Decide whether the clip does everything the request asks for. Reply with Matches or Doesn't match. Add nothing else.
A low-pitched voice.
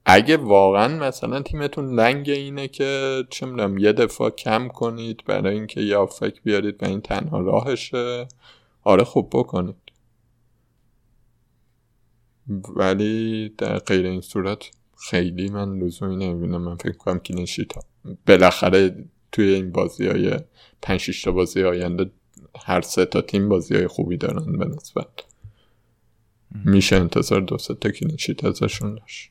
Matches